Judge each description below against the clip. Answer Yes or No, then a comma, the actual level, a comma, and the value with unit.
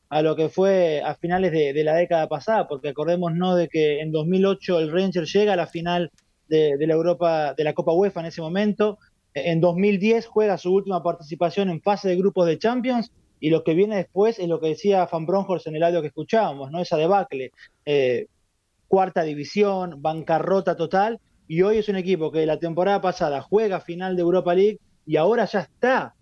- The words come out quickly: Yes, fast, 205 wpm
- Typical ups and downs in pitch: Yes, average, 3.4 semitones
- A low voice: No, medium, 175 Hz